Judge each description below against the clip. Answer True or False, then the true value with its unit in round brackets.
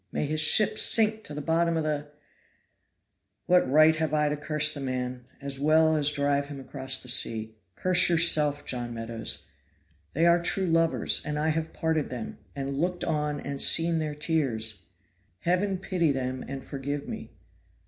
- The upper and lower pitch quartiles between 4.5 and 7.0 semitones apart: False (3.1 semitones)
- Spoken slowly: False (170 wpm)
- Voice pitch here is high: False (150 Hz)